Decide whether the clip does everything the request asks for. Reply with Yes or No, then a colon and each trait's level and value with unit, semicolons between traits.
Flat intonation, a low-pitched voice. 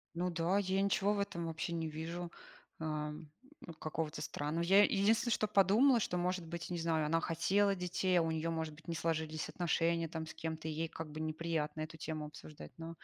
No: narrow, 2.2 semitones; medium, 165 Hz